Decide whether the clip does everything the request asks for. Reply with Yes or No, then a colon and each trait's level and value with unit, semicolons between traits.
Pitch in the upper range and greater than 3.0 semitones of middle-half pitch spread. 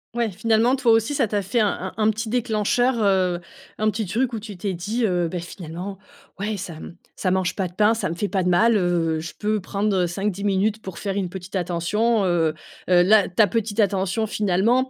Yes: high, 200 Hz; average, 3.4 semitones